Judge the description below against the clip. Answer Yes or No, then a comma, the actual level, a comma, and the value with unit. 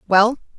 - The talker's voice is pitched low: No, high, 220 Hz